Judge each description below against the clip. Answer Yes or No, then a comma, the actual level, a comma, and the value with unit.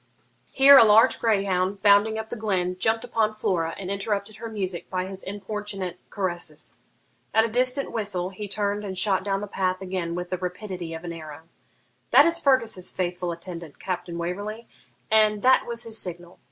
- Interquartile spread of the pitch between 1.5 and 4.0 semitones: Yes, average, 3.3 semitones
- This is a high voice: Yes, high, 195 Hz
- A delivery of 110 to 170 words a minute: No, average, 180 wpm